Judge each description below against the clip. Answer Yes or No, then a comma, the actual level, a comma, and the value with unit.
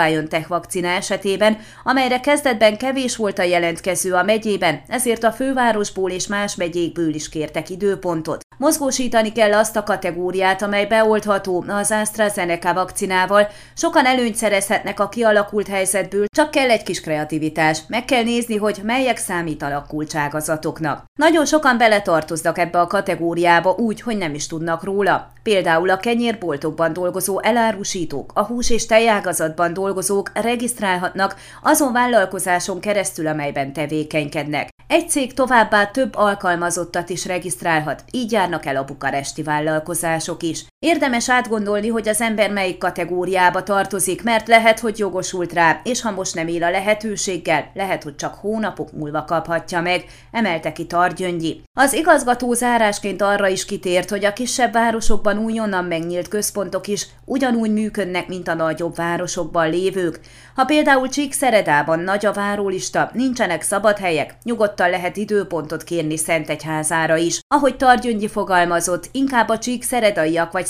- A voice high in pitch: Yes, high, 195 Hz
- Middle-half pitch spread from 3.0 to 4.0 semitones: No, average, 4.6 semitones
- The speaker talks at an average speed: Yes, average, 135 wpm